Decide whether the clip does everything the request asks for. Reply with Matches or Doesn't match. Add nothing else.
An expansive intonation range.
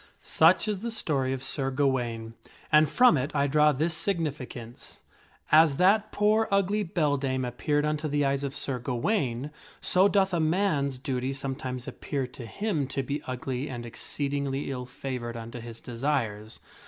Doesn't match